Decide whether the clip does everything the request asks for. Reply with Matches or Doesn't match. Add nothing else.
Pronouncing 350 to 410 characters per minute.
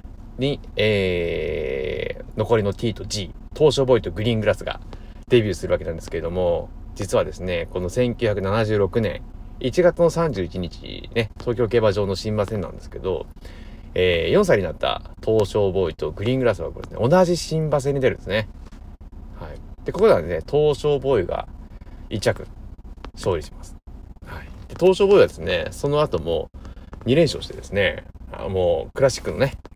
Doesn't match